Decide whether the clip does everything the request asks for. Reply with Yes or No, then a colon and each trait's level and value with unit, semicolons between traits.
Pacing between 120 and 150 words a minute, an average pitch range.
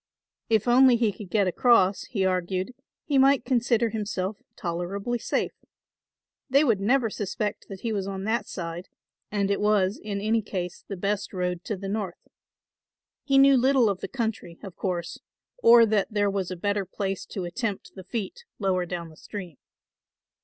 No: average, 175 wpm; average, 3.6 semitones